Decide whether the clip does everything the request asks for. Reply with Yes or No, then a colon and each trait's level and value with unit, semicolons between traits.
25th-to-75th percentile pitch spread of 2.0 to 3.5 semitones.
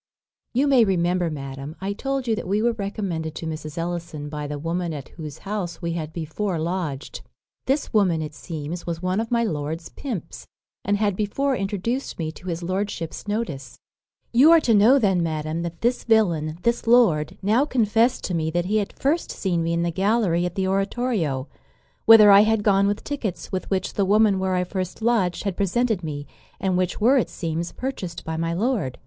No: average, 4.8 semitones